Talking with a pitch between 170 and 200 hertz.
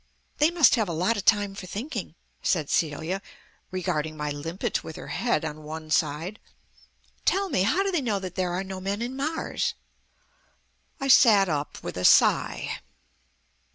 Yes: high, 190 Hz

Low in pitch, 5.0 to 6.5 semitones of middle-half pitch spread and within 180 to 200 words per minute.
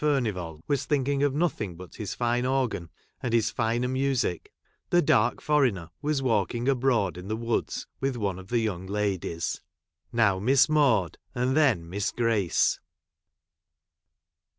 No: low, 120 Hz; wide, 5.5 semitones; average, 150 wpm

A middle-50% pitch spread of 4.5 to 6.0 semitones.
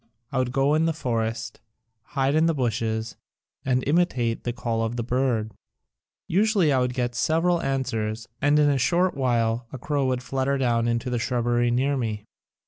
No: average, 3.2 semitones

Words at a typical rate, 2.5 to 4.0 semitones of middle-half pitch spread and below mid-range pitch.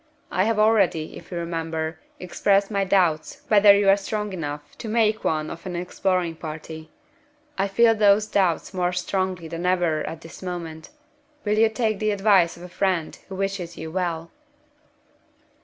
No: average, 170 wpm; average, 3.5 semitones; medium, 185 Hz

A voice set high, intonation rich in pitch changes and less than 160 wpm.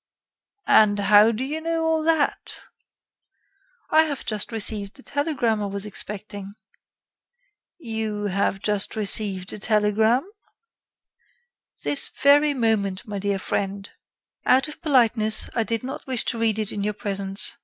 No: high, 215 Hz; average, 4.5 semitones; average, 140 wpm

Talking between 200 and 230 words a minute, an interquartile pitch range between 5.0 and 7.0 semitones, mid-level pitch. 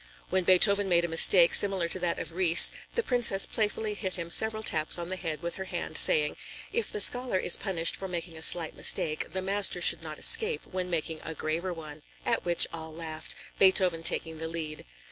No: fast, 205 wpm; average, 2.9 semitones; medium, 175 Hz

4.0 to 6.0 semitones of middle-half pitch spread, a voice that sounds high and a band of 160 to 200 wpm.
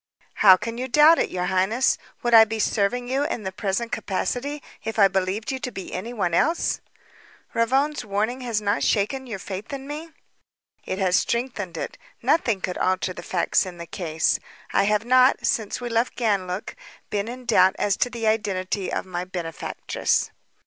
Yes: average, 4.6 semitones; high, 215 Hz; average, 180 wpm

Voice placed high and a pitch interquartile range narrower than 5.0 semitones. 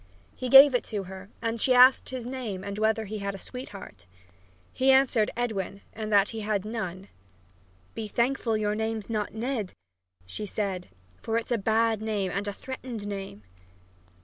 Yes: high, 220 Hz; average, 2.9 semitones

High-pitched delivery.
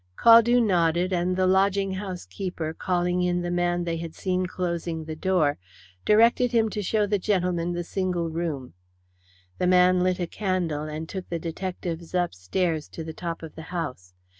No: medium, 180 Hz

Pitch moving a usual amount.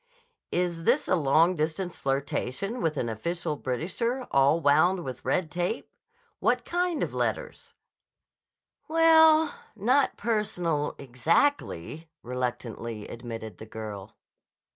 No: wide, 8.8 semitones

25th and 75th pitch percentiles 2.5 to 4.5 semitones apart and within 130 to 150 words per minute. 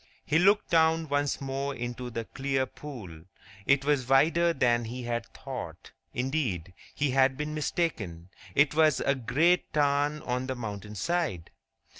Yes: average, 4.0 semitones; average, 145 wpm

